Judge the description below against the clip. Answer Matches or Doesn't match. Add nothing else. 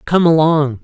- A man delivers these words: Matches